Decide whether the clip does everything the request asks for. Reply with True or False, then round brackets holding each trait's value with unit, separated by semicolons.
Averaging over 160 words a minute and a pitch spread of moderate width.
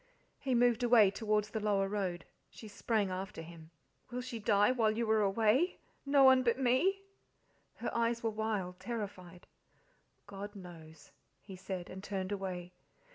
False (155 wpm; 3.7 semitones)